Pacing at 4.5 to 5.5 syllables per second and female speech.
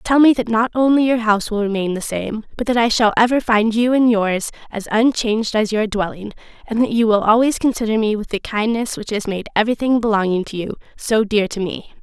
No: 5.7 syllables/s; female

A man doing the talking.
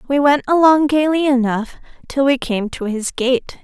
No: female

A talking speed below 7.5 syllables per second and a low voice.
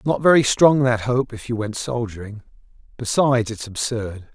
Yes: 4.9 syllables/s; low, 120 Hz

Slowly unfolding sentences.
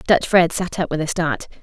No: fast, 260 wpm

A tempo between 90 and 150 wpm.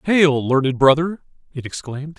Yes: slow, 135 wpm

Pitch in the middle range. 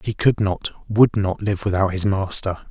No: low, 100 Hz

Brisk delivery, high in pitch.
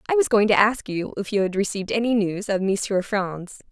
Yes: fast, 240 wpm; high, 205 Hz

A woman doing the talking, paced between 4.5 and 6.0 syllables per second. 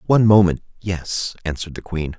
No: male; 5.6 syllables/s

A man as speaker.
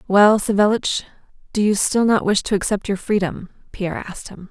No: female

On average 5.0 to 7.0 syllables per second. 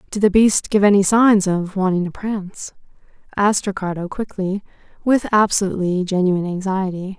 Yes: 5.5 syllables/s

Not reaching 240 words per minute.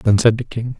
No: fast, 300 wpm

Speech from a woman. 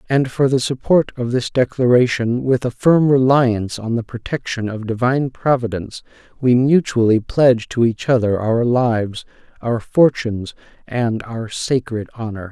No: male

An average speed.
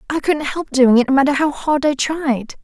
No: fast, 250 wpm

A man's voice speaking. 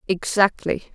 No: female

